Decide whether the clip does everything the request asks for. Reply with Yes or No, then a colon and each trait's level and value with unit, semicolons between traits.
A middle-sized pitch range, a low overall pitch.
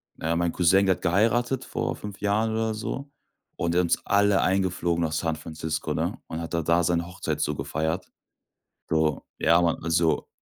Yes: average, 3.6 semitones; very low, 85 Hz